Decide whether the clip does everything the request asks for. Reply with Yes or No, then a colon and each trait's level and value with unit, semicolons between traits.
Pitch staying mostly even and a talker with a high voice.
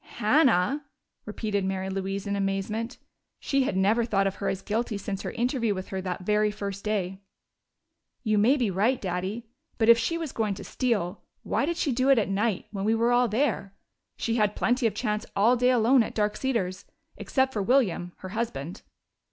No: average, 3.7 semitones; high, 210 Hz